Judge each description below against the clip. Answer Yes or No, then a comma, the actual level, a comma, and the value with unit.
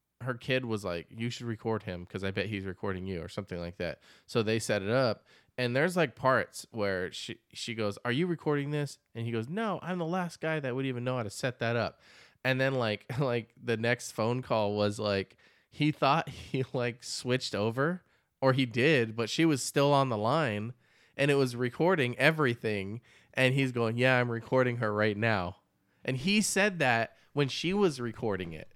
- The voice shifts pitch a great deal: No, average, 4.0 semitones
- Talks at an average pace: No, fast, 210 wpm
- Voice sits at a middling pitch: No, low, 125 Hz